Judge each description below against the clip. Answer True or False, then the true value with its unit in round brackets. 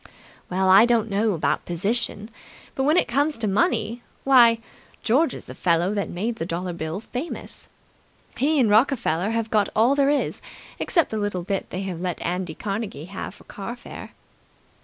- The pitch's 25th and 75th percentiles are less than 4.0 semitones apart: False (4.5 semitones)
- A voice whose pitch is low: False (210 Hz)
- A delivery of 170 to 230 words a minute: True (180 wpm)